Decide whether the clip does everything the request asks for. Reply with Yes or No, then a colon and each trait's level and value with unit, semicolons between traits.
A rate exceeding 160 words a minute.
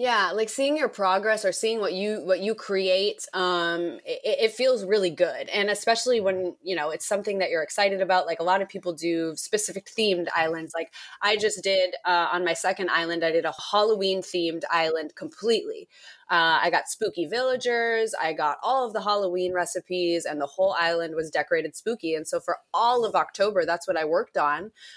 Yes: average, 200 wpm